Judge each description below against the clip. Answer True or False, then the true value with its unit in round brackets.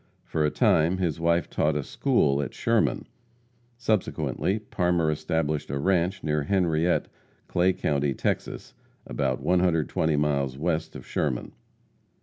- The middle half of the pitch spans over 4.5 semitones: False (3.3 semitones)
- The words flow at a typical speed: False (130 wpm)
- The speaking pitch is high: False (80 Hz)